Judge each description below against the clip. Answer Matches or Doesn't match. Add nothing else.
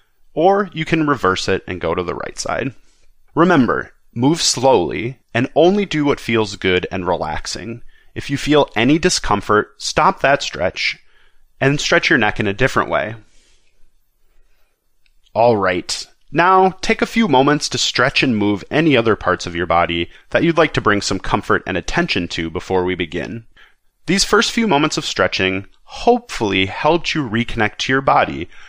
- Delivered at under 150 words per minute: Doesn't match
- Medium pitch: Doesn't match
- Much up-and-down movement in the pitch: Matches